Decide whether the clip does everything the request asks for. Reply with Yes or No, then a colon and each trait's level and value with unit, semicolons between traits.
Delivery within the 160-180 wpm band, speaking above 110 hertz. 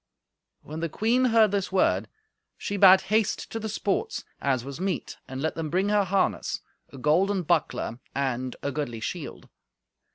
Yes: average, 165 wpm; medium, 185 Hz